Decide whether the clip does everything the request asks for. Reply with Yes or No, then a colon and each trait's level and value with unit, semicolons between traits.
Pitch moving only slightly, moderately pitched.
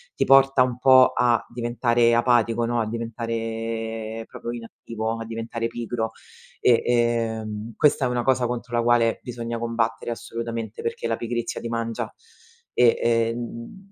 No: narrow, 0.9 semitones; low, 115 Hz